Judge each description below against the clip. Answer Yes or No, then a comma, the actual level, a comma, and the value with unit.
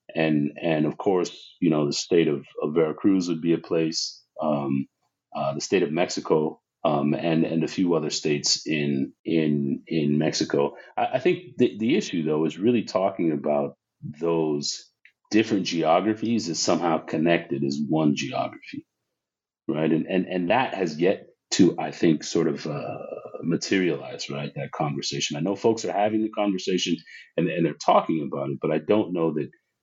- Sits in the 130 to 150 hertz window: No, very low, 80 Hz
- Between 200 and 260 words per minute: No, average, 175 wpm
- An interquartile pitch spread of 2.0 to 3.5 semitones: No, average, 3.9 semitones